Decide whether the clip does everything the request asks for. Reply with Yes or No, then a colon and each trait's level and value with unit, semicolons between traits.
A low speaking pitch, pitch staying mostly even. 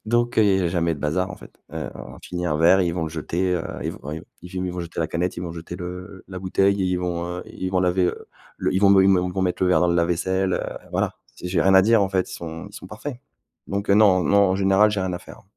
Yes: very low, 90 Hz; narrow, 1.8 semitones